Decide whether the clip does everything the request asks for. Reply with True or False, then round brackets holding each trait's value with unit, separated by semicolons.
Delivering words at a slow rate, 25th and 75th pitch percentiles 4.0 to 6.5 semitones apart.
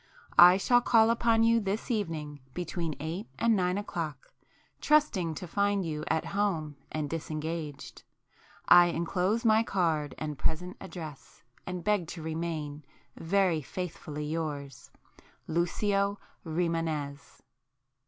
True (120 wpm; 4.3 semitones)